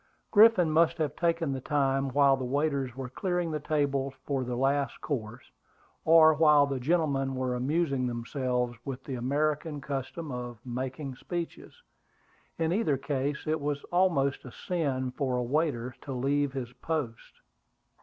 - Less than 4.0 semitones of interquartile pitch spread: Yes, average, 3.2 semitones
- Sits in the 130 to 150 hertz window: Yes, medium, 140 Hz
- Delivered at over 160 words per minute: No, average, 155 wpm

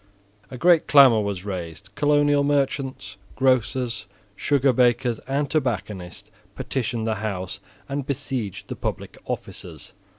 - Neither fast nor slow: No, slow, 120 wpm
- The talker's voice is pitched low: Yes, low, 125 Hz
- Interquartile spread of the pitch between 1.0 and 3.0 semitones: No, average, 5.3 semitones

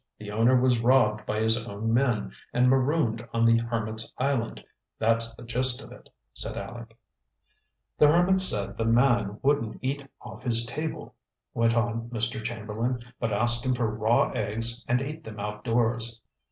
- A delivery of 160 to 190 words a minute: Yes, average, 165 wpm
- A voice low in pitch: Yes, low, 115 Hz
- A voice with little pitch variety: Yes, narrow, 2.2 semitones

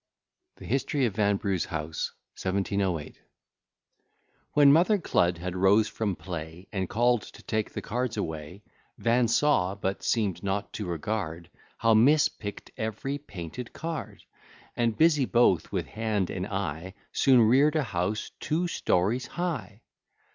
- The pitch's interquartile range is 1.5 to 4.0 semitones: No, average, 5.2 semitones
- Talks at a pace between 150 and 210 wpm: No, average, 140 wpm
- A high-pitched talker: No, low, 105 Hz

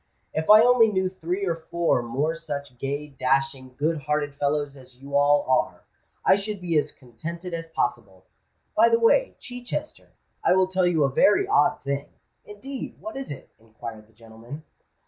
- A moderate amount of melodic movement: No, wide, 5.8 semitones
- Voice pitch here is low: No, medium, 150 Hz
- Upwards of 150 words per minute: Yes, average, 175 wpm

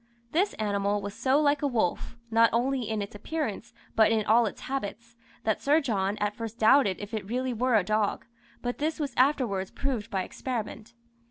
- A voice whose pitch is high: Yes, high, 230 Hz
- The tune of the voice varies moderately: Yes, average, 4.2 semitones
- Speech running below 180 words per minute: No, average, 190 wpm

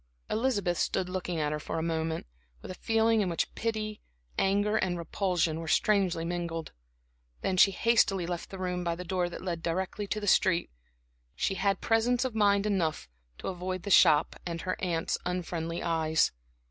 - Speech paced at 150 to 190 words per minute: Yes, average, 180 wpm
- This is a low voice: No, medium, 180 Hz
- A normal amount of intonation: Yes, average, 3.2 semitones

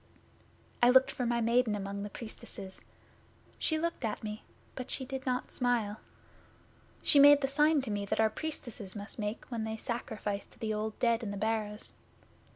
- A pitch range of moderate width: Yes, average, 3.5 semitones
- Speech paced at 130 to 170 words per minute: No, average, 180 wpm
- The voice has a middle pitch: No, high, 225 Hz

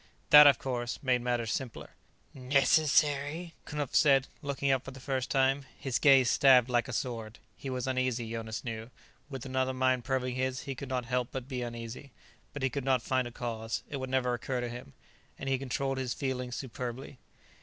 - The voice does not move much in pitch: Yes, narrow, 1.8 semitones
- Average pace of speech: Yes, average, 195 wpm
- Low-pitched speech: Yes, low, 130 Hz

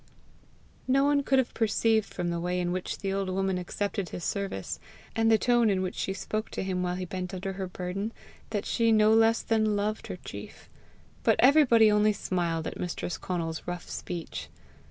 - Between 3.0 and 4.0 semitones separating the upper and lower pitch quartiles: Yes, average, 3.5 semitones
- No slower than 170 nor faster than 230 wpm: Yes, average, 195 wpm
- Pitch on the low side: No, high, 195 Hz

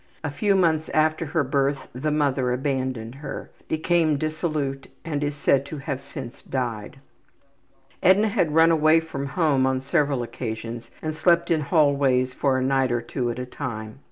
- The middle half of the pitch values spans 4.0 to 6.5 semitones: No, average, 3.3 semitones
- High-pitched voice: No, medium, 140 Hz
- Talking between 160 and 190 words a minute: Yes, average, 170 wpm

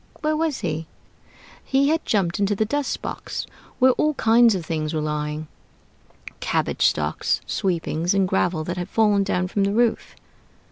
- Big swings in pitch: Yes, wide, 5.9 semitones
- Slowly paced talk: No, average, 160 wpm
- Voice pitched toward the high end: Yes, high, 195 Hz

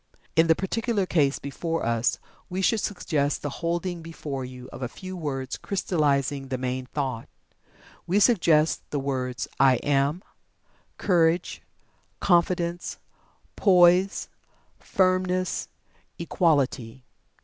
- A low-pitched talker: No, medium, 160 Hz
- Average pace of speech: No, slow, 110 wpm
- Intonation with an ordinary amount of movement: Yes, average, 5.0 semitones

